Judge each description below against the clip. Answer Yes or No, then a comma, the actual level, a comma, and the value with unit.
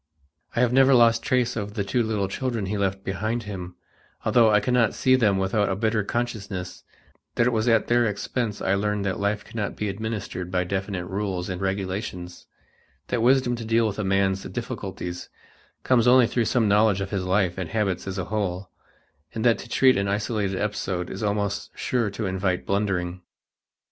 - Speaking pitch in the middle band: No, low, 105 Hz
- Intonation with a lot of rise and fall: No, average, 3.1 semitones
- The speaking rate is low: No, average, 190 wpm